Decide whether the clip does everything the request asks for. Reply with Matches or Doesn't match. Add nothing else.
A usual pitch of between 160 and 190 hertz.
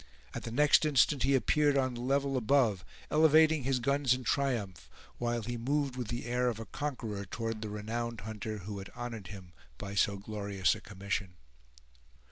Doesn't match